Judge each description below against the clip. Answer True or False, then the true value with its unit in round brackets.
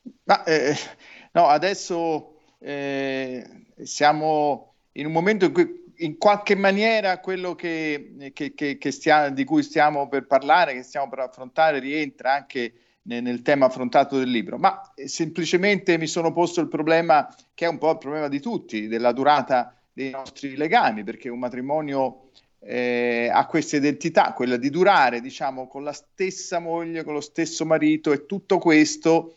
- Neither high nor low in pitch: True (150 Hz)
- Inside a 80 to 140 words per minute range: False (165 wpm)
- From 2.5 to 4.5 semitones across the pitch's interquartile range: True (3.9 semitones)